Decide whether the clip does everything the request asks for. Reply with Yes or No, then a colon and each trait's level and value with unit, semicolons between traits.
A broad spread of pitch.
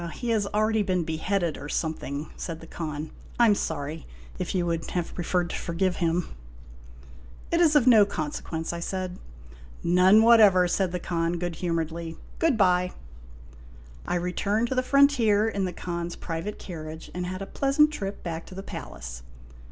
No: average, 3.8 semitones